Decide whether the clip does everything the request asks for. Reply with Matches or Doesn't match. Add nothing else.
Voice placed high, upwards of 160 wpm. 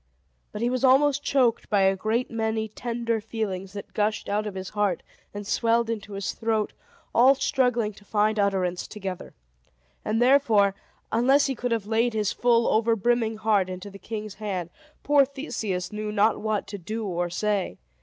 Matches